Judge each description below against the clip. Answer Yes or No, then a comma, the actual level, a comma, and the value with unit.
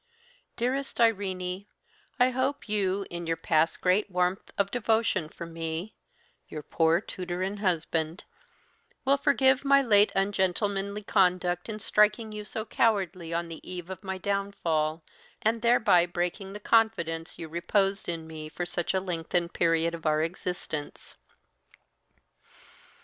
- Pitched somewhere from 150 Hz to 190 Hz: Yes, medium, 185 Hz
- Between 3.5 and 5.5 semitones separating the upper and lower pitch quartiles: Yes, average, 3.9 semitones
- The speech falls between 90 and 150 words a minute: Yes, average, 140 wpm